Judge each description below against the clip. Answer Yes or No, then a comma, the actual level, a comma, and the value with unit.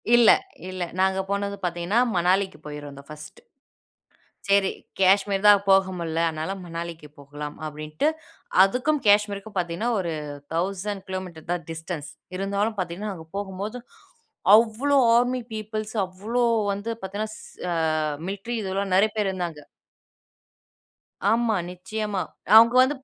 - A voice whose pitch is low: No, high, 195 Hz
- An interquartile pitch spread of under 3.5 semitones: No, average, 3.8 semitones